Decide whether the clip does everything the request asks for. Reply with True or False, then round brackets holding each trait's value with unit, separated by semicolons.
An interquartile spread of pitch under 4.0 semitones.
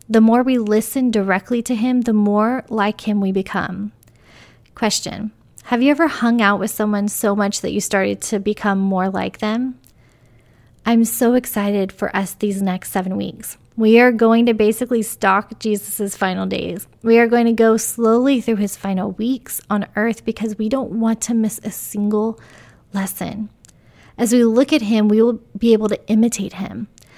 True (2.5 semitones)